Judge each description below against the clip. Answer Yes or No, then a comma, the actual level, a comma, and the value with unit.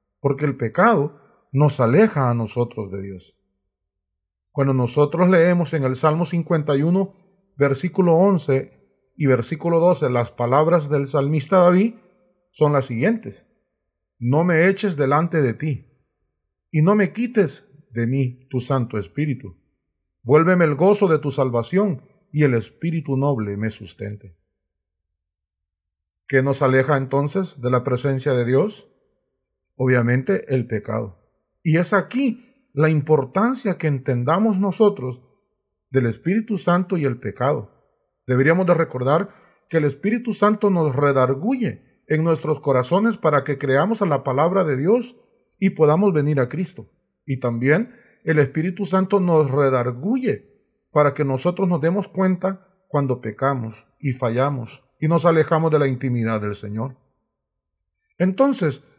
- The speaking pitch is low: No, medium, 145 Hz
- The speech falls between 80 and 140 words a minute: Yes, average, 135 wpm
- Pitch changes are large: Yes, wide, 6.3 semitones